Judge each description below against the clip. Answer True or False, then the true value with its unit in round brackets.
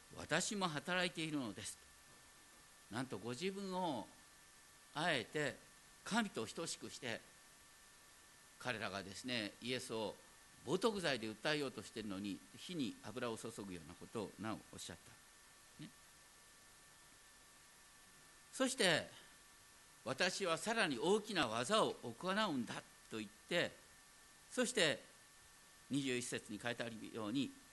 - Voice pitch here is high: False (135 Hz)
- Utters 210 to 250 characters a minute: True (235 characters per minute)